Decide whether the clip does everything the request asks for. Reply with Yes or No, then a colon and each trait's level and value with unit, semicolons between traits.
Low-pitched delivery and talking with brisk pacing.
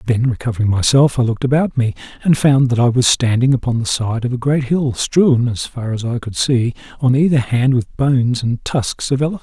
Yes: low, 125 Hz; fast, 230 wpm